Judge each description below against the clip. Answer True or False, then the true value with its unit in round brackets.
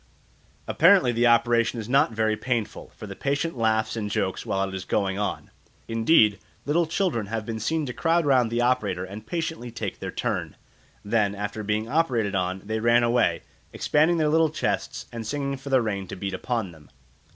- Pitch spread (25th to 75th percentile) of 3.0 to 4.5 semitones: False (4.9 semitones)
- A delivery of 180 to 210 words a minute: True (190 wpm)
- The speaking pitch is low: True (115 Hz)